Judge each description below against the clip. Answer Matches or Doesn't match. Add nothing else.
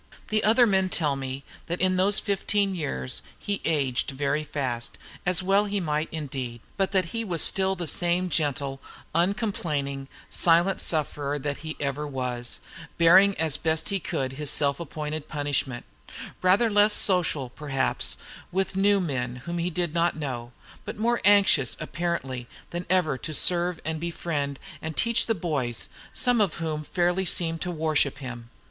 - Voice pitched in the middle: Matches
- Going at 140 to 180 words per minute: Matches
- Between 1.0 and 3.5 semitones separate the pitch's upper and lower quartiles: Doesn't match